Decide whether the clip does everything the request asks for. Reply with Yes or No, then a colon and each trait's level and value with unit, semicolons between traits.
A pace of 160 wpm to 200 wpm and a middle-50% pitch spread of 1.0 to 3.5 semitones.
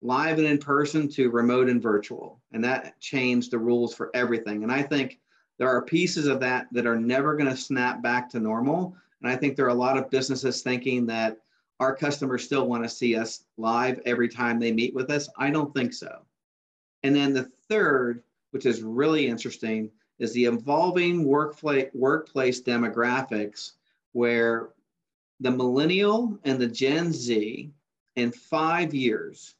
Yes: average, 170 wpm; average, 3.0 semitones